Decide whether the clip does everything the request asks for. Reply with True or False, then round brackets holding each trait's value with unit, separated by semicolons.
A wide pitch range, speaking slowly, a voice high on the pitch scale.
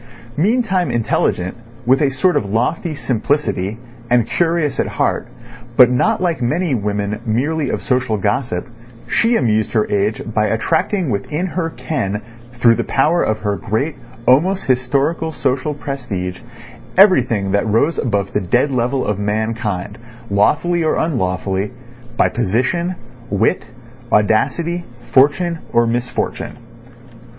False (7.0 semitones; 130 wpm; 125 Hz)